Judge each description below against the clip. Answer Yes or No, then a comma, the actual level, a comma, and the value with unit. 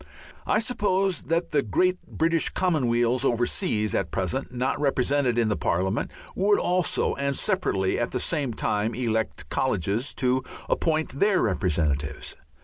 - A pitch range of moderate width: No, wide, 7.3 semitones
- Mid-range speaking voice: No, low, 130 Hz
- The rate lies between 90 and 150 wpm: Yes, average, 140 wpm